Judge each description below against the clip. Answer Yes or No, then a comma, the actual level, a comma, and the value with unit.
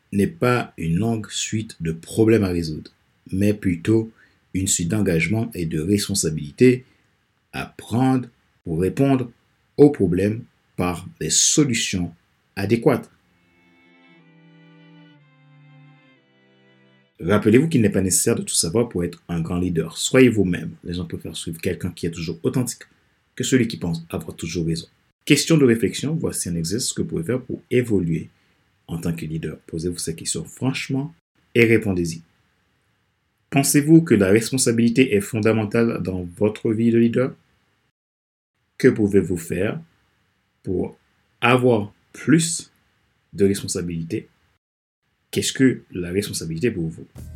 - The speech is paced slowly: Yes, slow, 135 wpm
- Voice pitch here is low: Yes, low, 105 Hz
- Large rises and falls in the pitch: Yes, wide, 6.0 semitones